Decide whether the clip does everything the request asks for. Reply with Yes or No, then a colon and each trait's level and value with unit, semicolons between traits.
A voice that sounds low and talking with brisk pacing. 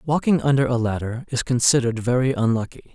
No: low, 125 Hz; average, 165 wpm